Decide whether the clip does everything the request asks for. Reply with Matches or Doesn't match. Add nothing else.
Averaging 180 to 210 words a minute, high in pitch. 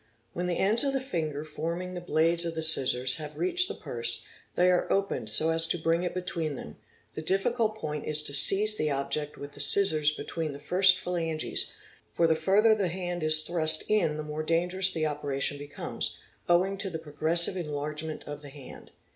Doesn't match